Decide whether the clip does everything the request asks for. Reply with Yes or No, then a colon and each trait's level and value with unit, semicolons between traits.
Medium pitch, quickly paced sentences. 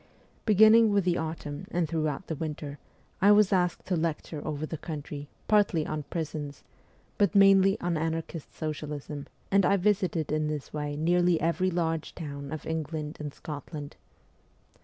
No: medium, 160 Hz; average, 155 wpm